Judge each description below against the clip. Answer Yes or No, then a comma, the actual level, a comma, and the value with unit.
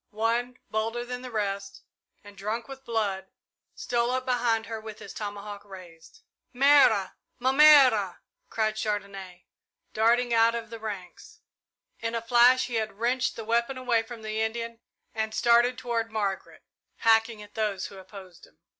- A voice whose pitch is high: Yes, high, 225 Hz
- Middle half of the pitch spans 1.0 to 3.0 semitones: Yes, average, 2.7 semitones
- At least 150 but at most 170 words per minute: Yes, average, 155 wpm